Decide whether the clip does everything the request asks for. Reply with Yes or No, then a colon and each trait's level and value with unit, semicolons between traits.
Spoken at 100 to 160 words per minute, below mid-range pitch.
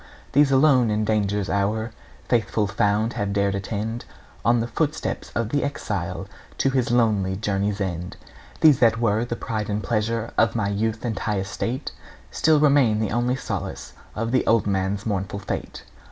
No: average, 170 wpm; low, 110 Hz